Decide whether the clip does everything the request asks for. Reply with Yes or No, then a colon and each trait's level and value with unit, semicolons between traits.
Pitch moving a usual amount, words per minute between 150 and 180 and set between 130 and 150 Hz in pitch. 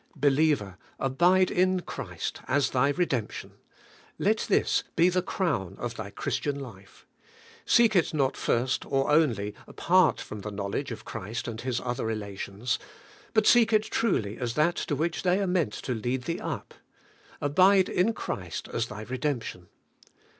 No: wide, 8.0 semitones; average, 155 wpm; low, 135 Hz